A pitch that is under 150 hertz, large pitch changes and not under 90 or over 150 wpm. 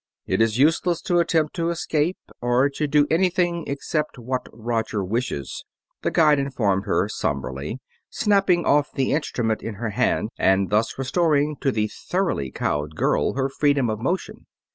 No: low, 135 Hz; wide, 6.2 semitones; average, 160 wpm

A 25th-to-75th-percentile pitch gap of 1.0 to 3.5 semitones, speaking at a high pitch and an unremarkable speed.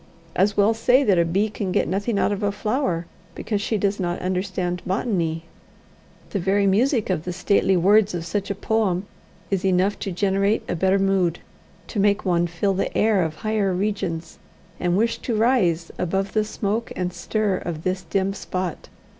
Yes: narrow, 2.6 semitones; high, 195 Hz; average, 185 wpm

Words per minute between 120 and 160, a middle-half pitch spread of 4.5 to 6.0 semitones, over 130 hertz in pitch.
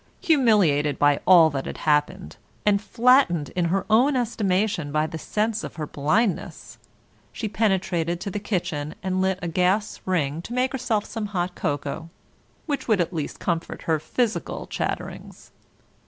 Yes: average, 155 wpm; average, 5.2 semitones; medium, 185 Hz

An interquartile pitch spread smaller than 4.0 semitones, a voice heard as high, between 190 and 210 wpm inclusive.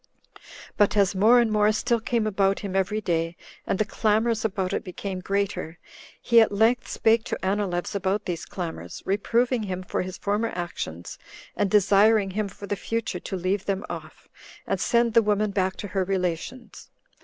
No: narrow, 2.6 semitones; high, 200 Hz; average, 180 wpm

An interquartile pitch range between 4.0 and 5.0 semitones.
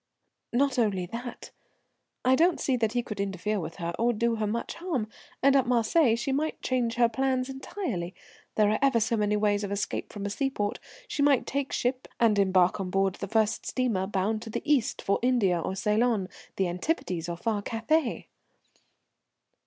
Yes: average, 4.3 semitones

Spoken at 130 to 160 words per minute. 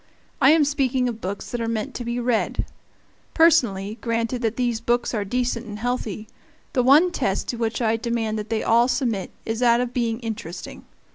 No: average, 195 wpm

